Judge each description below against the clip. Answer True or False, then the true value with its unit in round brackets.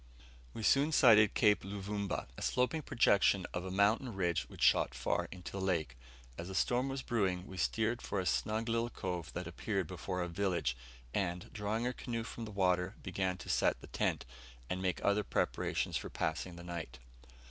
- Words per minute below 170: False (190 wpm)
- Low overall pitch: True (95 Hz)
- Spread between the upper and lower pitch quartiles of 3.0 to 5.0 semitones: True (3.7 semitones)